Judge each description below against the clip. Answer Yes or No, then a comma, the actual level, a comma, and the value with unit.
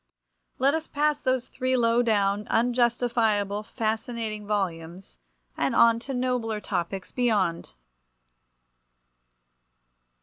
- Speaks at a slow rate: Yes, slow, 95 wpm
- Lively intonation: No, average, 3.3 semitones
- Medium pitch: No, high, 230 Hz